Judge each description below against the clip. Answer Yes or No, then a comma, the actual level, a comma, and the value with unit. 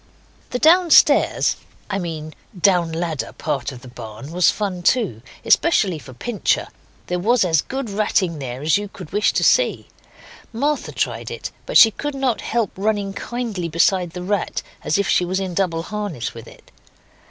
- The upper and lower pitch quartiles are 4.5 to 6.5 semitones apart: Yes, average, 4.9 semitones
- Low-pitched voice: No, medium, 185 Hz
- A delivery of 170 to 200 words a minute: Yes, average, 175 wpm